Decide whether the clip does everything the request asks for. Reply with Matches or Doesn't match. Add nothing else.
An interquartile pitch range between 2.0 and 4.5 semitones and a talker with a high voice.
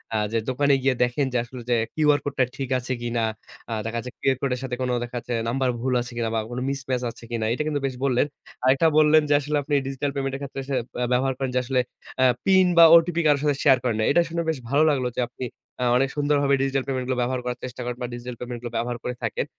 Doesn't match